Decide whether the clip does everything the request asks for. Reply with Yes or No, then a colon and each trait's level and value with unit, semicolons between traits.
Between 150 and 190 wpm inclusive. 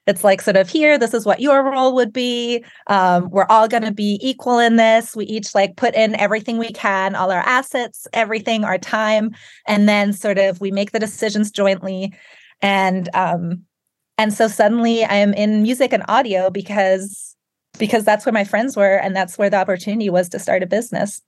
No: fast, 205 wpm